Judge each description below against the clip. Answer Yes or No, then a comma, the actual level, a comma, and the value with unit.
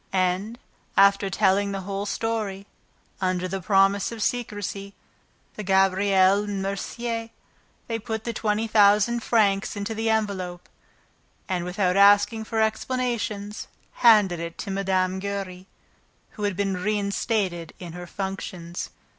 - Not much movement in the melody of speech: Yes, narrow, 2.3 semitones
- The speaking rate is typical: No, slow, 130 wpm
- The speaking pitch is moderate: No, high, 200 Hz